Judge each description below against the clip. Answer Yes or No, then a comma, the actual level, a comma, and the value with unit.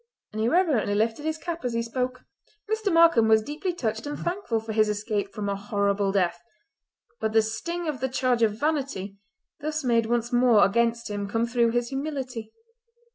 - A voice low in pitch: No, high, 235 Hz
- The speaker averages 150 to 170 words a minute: No, average, 185 wpm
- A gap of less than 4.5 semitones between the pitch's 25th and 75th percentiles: No, average, 4.9 semitones